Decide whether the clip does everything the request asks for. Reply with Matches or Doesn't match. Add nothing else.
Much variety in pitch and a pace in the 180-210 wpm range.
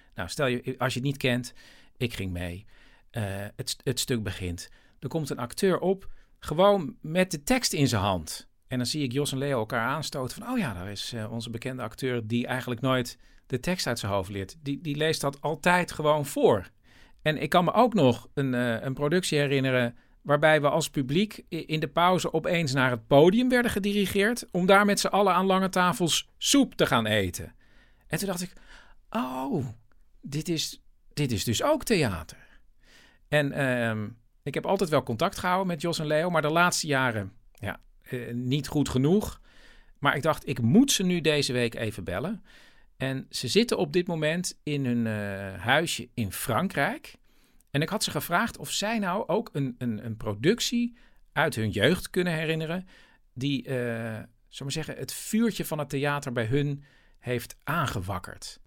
Matches